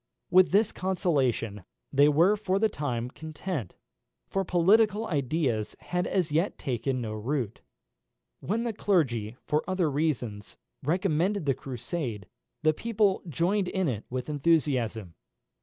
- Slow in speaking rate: Yes, slow, 130 wpm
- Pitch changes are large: Yes, wide, 7.0 semitones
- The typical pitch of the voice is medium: Yes, medium, 155 Hz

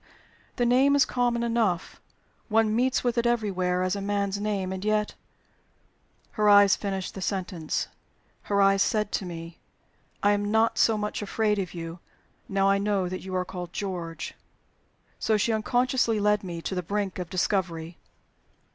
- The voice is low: No, high, 200 Hz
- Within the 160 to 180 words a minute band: Yes, average, 170 wpm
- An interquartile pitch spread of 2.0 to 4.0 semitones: Yes, average, 2.8 semitones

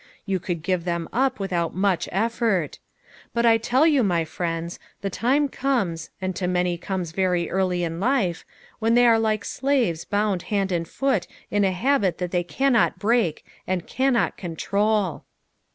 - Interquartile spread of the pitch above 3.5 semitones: Yes, average, 4.8 semitones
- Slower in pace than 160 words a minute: No, average, 170 wpm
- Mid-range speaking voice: No, high, 195 Hz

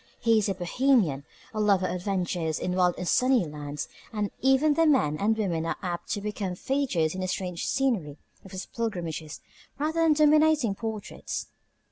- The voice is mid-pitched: No, high, 200 Hz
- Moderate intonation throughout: No, wide, 6.6 semitones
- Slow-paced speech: No, average, 175 wpm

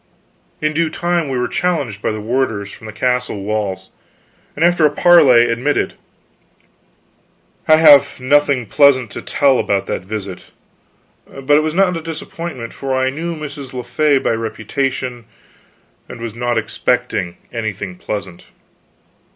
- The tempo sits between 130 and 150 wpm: Yes, average, 145 wpm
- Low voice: Yes, low, 130 Hz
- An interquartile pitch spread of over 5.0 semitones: Yes, wide, 5.5 semitones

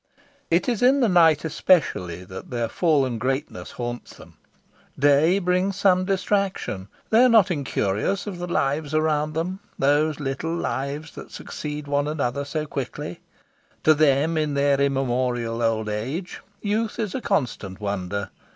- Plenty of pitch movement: Yes, wide, 5.8 semitones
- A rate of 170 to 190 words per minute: No, average, 150 wpm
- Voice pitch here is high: No, medium, 150 Hz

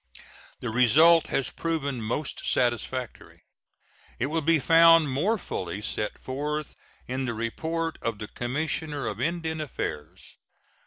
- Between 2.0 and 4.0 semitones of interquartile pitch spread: No, wide, 5.4 semitones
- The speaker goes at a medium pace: No, slow, 125 wpm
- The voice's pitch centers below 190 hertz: Yes, medium, 140 Hz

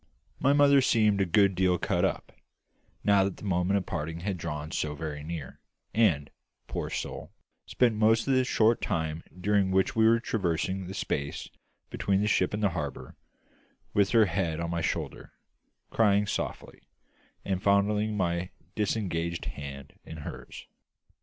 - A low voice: Yes, very low, 95 Hz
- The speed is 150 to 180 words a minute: Yes, average, 160 wpm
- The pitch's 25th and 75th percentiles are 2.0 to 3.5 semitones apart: No, average, 4.2 semitones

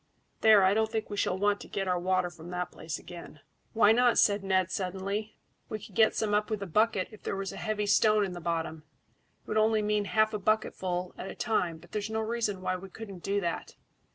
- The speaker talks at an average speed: No, fast, 235 wpm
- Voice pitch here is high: Yes, high, 200 Hz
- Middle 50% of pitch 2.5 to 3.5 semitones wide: Yes, average, 2.9 semitones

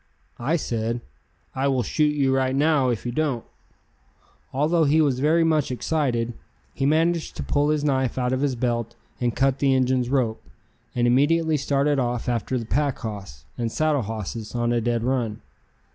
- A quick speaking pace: No, average, 175 wpm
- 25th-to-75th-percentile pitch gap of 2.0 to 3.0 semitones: No, average, 3.6 semitones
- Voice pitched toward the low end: Yes, low, 130 Hz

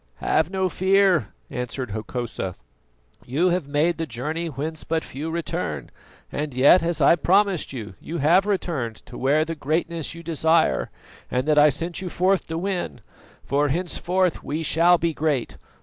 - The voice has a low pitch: No, medium, 160 Hz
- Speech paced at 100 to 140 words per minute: No, average, 165 wpm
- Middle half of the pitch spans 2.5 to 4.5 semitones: Yes, average, 3.5 semitones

